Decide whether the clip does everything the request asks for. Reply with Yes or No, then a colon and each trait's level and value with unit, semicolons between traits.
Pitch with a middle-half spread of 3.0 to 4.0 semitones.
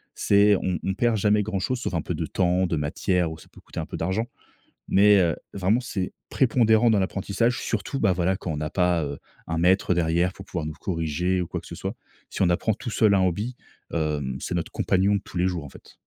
Yes: average, 3.5 semitones